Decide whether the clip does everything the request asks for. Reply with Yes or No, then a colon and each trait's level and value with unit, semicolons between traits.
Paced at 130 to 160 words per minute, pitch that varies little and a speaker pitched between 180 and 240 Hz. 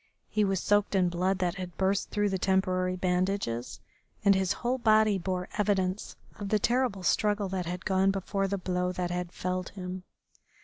No: average, 180 wpm; narrow, 1.7 semitones; high, 190 Hz